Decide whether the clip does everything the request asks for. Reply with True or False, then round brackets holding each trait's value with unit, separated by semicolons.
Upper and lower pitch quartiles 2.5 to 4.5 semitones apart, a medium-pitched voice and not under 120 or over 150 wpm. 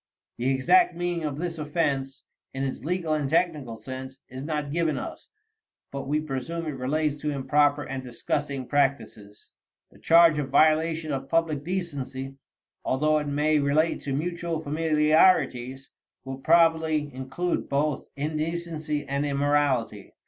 True (2.9 semitones; 150 Hz; 140 wpm)